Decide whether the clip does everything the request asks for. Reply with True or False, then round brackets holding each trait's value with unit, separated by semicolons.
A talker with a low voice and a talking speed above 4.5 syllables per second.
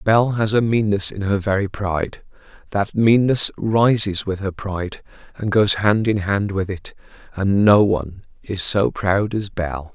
False (100 Hz; 4.3 syllables/s)